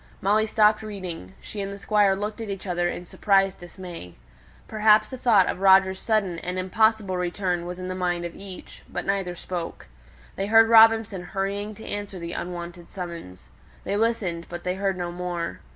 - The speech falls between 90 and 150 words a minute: No, average, 185 wpm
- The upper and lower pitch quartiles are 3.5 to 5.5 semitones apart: No, average, 2.9 semitones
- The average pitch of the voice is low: No, high, 190 Hz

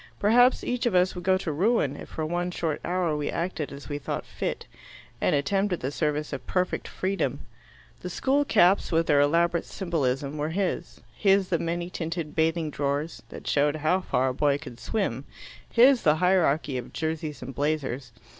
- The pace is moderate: Yes, average, 185 wpm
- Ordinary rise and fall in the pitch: Yes, average, 4.2 semitones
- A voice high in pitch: No, medium, 160 Hz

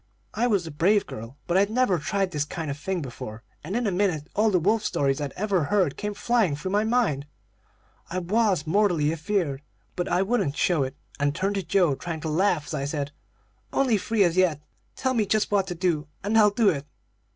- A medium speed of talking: No, fast, 220 wpm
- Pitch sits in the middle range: Yes, medium, 180 Hz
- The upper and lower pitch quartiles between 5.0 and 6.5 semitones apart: Yes, wide, 5.5 semitones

